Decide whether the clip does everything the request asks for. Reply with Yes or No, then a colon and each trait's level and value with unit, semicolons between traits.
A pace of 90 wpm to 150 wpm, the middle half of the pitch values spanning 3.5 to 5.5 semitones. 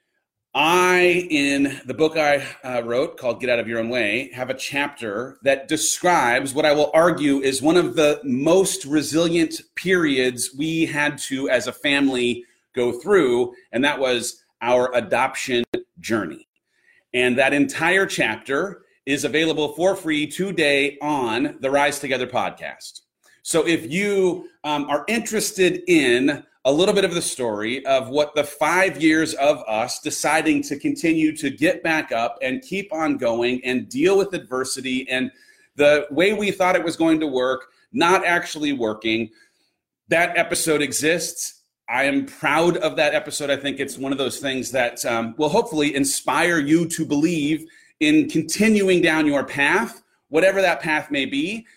No: average, 160 wpm; average, 4.9 semitones